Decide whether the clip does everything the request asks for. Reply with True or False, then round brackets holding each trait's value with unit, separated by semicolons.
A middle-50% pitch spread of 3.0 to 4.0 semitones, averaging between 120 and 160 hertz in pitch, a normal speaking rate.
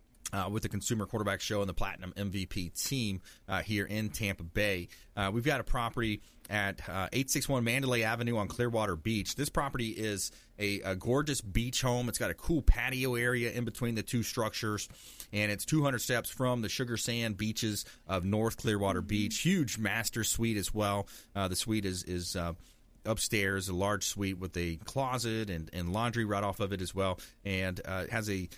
False (3.3 semitones; 105 Hz; 195 wpm)